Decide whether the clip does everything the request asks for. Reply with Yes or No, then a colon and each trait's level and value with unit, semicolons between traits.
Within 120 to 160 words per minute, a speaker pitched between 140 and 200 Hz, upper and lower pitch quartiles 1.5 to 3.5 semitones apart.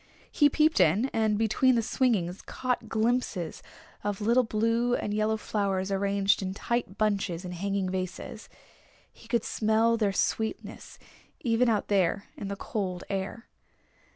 No: average, 145 wpm; high, 215 Hz; average, 2.9 semitones